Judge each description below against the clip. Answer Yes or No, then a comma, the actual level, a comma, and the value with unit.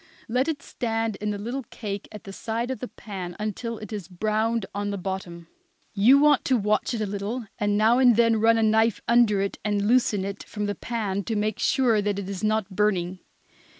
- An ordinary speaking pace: No, fast, 215 wpm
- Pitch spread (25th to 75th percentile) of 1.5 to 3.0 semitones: Yes, narrow, 2.4 semitones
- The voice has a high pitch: Yes, high, 215 Hz